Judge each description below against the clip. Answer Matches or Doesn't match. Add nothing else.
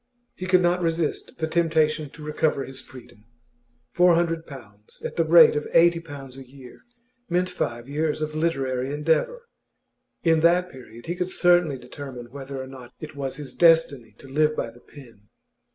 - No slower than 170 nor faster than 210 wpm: Matches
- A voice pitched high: Doesn't match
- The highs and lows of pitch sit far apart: Doesn't match